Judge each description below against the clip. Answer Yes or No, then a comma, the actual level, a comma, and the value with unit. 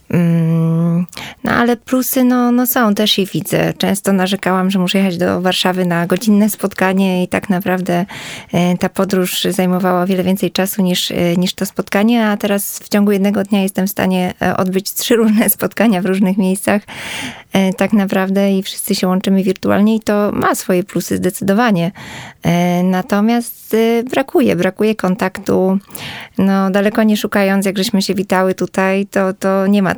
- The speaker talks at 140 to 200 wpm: Yes, average, 155 wpm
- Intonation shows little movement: Yes, narrow, 2.1 semitones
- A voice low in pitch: No, high, 195 Hz